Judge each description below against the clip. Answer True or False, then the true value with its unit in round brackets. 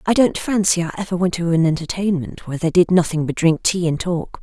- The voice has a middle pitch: True (175 Hz)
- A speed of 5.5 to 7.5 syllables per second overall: True (5.9 syllables/s)